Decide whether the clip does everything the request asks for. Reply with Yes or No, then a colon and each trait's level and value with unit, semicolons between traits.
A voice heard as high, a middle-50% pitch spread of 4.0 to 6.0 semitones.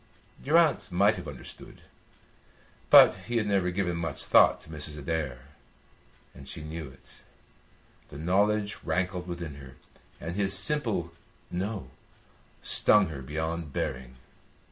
No: very low, 85 Hz; average, 4.8 semitones